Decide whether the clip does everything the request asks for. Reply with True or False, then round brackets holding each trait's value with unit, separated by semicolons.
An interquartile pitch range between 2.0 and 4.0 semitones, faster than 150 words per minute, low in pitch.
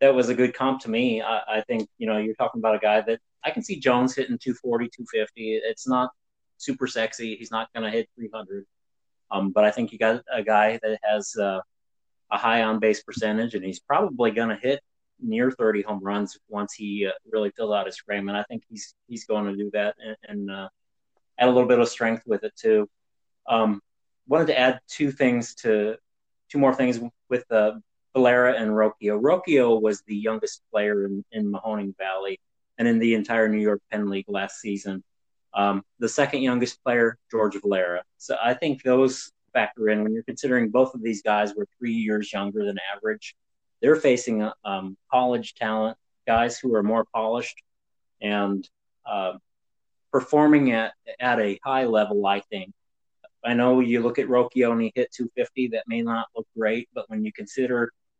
True (2.9 semitones; 195 wpm; 110 Hz)